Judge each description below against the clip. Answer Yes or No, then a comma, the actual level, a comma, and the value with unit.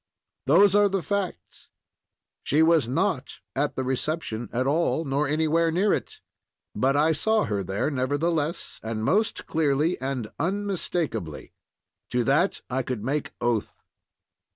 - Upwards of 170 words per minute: No, slow, 135 wpm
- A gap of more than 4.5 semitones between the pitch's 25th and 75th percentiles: Yes, average, 4.9 semitones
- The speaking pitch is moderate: Yes, medium, 150 Hz